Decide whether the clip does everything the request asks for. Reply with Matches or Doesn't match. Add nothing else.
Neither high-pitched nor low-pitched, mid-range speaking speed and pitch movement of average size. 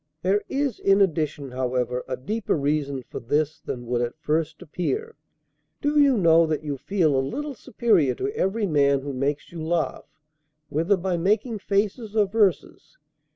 Doesn't match